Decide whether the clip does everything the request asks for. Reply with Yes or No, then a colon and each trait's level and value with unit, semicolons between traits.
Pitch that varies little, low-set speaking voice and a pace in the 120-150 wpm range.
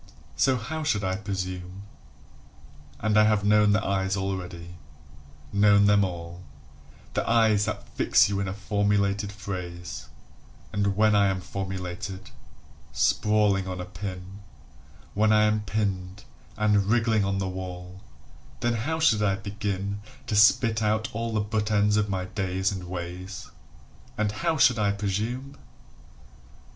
Yes: narrow, 2.1 semitones; low, 100 Hz; average, 145 wpm